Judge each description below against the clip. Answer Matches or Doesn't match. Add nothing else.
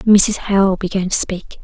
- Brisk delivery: Doesn't match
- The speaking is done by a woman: Matches